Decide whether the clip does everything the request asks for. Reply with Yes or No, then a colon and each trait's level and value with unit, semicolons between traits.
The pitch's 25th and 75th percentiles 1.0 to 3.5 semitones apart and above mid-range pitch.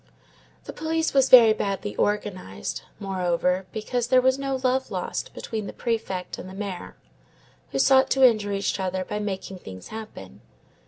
No: average, 5.2 semitones; high, 210 Hz